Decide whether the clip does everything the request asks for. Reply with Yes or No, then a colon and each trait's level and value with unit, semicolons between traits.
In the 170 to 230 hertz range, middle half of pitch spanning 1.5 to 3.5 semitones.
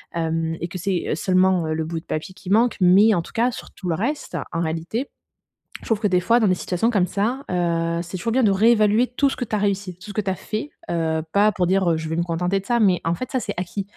No: high, 190 Hz; average, 4.1 semitones